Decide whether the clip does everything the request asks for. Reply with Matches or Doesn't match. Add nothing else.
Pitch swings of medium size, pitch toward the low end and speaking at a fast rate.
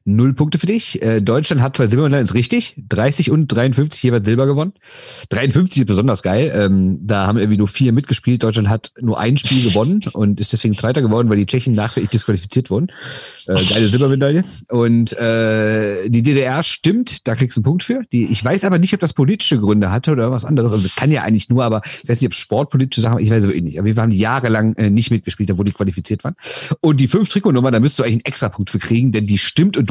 Matches